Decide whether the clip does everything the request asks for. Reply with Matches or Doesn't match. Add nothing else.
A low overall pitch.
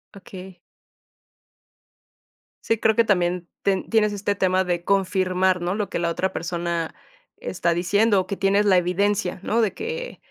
Doesn't match